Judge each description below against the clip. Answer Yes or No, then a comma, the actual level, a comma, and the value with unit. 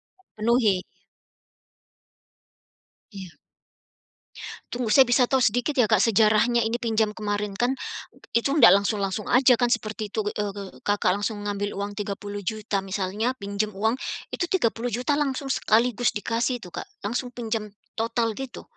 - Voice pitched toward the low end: No, high, 220 Hz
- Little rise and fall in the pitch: No, average, 3.0 semitones